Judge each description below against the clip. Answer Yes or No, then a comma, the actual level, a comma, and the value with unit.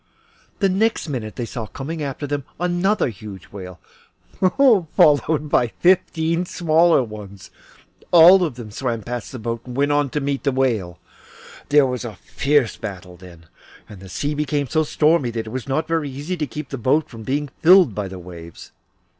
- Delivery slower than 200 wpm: Yes, average, 180 wpm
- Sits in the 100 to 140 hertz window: Yes, low, 135 Hz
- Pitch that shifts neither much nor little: No, wide, 6.1 semitones